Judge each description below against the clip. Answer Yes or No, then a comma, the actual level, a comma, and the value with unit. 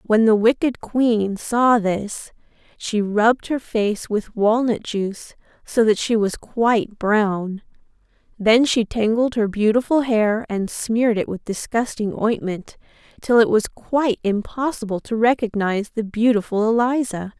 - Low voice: No, high, 220 Hz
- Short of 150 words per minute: Yes, average, 140 wpm